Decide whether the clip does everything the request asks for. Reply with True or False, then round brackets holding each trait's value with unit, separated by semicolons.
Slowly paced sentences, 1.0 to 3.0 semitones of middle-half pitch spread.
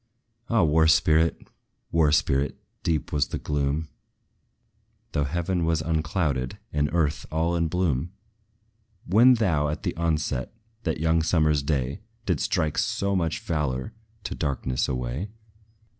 True (130 wpm; 2.5 semitones)